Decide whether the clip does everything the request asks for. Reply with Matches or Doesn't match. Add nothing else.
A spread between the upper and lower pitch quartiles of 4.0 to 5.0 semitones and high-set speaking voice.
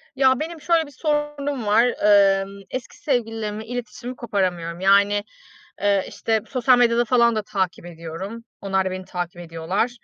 Matches